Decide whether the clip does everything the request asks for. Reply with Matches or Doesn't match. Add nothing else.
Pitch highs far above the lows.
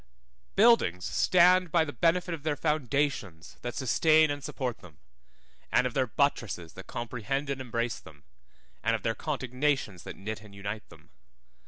Matches